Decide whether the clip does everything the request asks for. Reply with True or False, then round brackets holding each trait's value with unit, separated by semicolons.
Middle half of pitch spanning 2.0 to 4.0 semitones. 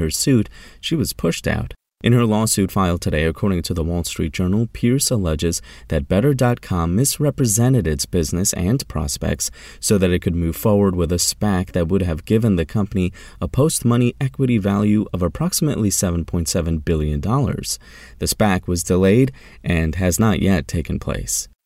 False (4.7 semitones)